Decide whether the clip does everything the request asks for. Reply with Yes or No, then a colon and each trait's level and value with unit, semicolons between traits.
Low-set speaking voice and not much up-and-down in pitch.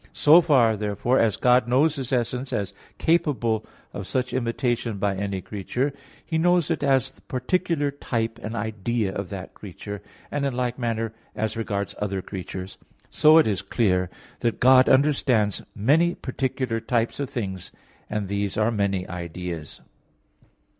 No: low, 115 Hz; average, 4.6 semitones